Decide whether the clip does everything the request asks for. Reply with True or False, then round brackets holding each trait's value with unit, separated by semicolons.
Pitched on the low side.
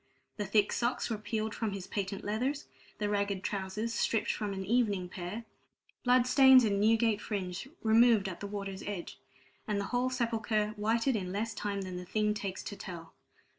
False (210 Hz)